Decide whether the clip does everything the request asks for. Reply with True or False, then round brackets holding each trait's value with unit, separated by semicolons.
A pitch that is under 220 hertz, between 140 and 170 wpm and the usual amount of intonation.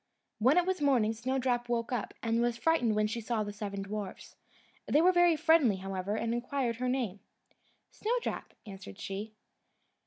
False (235 Hz; 165 wpm; 4.1 semitones)